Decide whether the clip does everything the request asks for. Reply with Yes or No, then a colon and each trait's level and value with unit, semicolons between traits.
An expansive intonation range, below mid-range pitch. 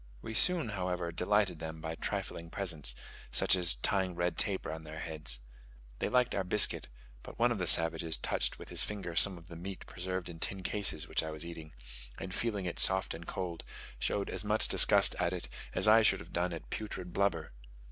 No: average, 3.1 semitones; very low, 90 Hz